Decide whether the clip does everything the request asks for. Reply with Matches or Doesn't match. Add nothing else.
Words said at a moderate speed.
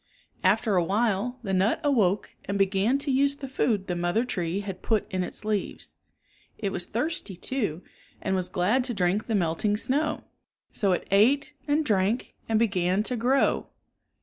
Matches